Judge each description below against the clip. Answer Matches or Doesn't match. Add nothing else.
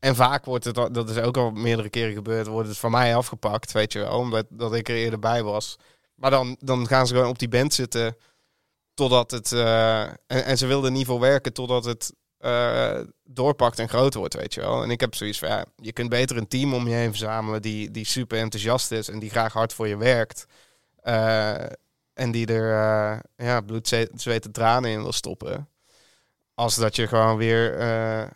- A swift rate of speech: Matches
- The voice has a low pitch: Matches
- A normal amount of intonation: Doesn't match